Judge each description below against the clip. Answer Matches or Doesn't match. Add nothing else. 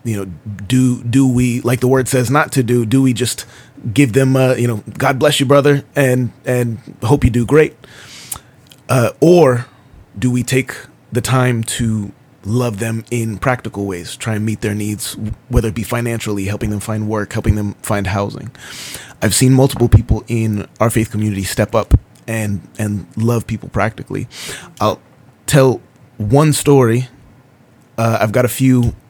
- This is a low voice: Matches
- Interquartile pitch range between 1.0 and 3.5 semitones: Matches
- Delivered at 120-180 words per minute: Matches